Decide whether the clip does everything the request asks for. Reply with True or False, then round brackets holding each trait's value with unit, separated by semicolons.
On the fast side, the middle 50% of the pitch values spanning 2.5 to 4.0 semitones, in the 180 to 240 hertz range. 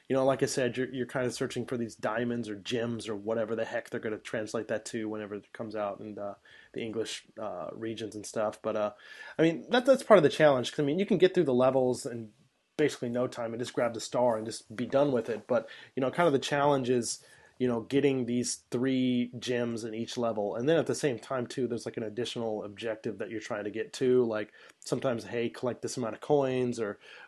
False (255 wpm; 2.9 semitones; 120 Hz)